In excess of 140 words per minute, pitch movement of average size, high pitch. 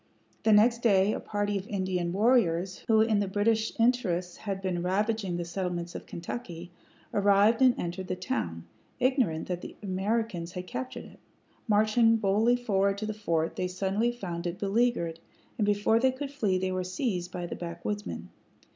Yes: average, 175 wpm; average, 3.8 semitones; high, 200 Hz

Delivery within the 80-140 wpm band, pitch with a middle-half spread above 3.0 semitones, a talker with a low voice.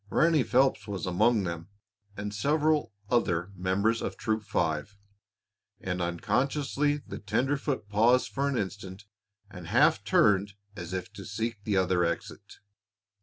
Yes: slow, 135 wpm; wide, 5.4 semitones; low, 105 Hz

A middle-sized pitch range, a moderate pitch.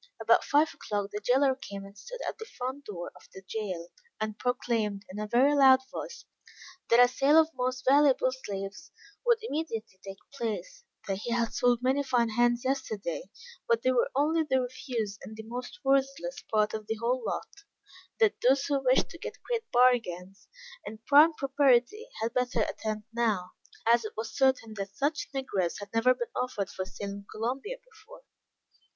No: average, 4.3 semitones; high, 245 Hz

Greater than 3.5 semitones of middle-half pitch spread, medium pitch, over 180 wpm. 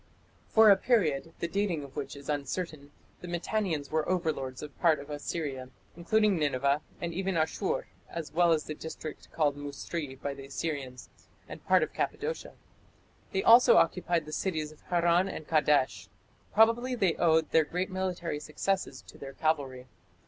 No: average, 4.1 semitones; medium, 160 Hz; average, 165 wpm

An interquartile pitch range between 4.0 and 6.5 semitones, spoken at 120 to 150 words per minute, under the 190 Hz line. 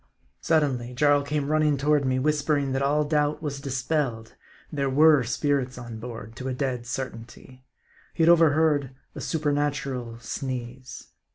No: average, 2.8 semitones; average, 145 wpm; medium, 140 Hz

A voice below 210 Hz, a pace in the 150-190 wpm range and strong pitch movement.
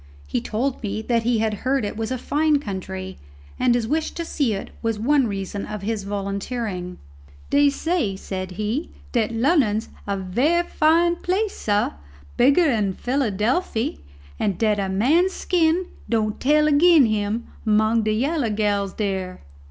No: high, 225 Hz; average, 160 wpm; wide, 5.8 semitones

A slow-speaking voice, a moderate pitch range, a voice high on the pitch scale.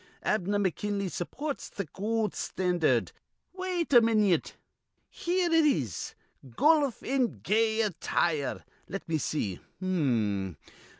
No: slow, 110 wpm; wide, 7.7 semitones; high, 205 Hz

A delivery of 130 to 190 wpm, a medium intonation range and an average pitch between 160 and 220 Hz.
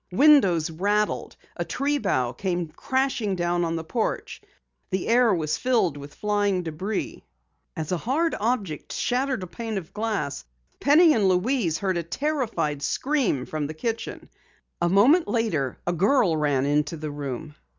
No: average, 155 wpm; wide, 7.1 semitones; high, 190 Hz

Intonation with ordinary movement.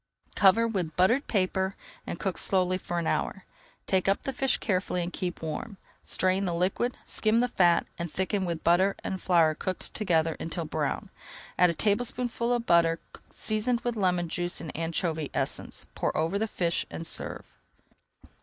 Yes: average, 3.4 semitones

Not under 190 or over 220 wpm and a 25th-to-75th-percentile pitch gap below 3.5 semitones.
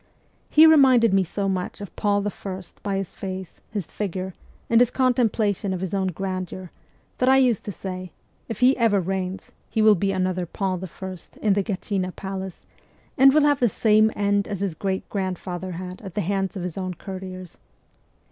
Yes: average, 195 wpm; narrow, 2.5 semitones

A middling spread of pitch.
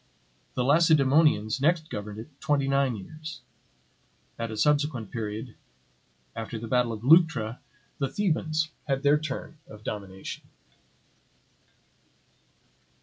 No: wide, 5.8 semitones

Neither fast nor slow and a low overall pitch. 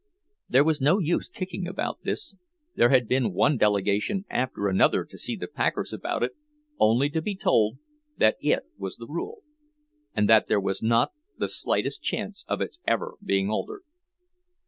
Yes: average, 170 wpm; low, 130 Hz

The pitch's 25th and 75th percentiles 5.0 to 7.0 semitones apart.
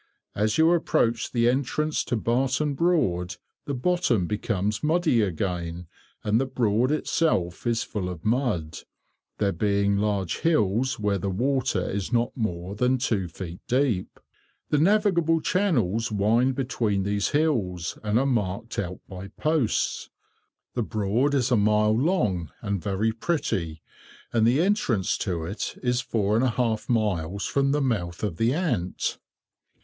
Yes: average, 5.3 semitones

